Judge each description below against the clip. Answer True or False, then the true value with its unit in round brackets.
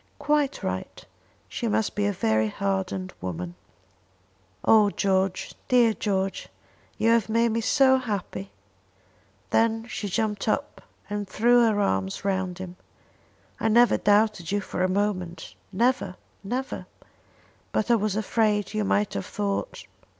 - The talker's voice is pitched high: True (205 Hz)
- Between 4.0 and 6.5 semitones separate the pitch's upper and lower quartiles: False (3.2 semitones)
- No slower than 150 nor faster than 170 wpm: False (135 wpm)